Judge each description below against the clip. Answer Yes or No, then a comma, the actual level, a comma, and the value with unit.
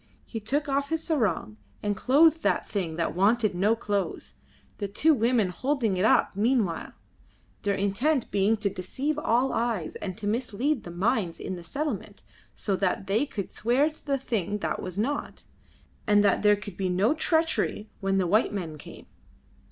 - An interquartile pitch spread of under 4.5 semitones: No, wide, 5.5 semitones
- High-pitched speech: Yes, high, 215 Hz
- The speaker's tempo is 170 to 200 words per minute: Yes, average, 175 wpm